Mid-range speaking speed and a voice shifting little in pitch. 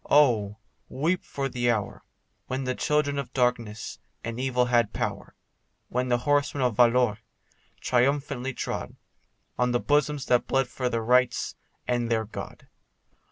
Yes: average, 145 wpm; narrow, 2.3 semitones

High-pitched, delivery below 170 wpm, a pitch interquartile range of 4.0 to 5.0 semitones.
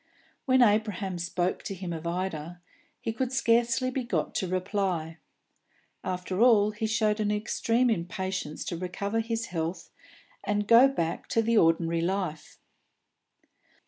Yes: high, 200 Hz; average, 140 wpm; average, 4.5 semitones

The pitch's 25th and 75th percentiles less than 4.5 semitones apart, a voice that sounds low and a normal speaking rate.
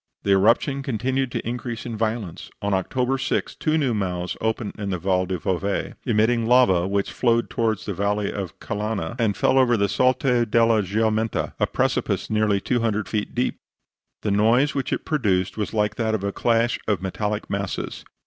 Yes: average, 3.0 semitones; low, 110 Hz; average, 180 wpm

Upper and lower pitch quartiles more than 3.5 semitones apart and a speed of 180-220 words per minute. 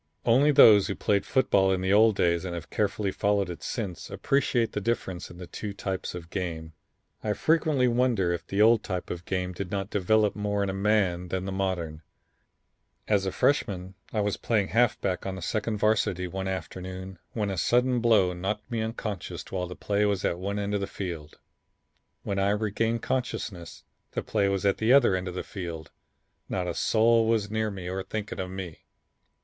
No: average, 2.9 semitones; average, 200 wpm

